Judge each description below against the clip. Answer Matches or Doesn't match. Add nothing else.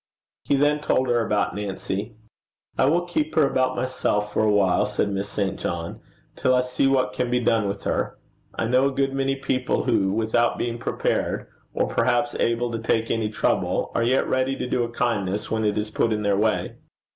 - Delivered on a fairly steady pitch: Doesn't match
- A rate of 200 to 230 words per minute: Matches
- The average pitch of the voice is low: Matches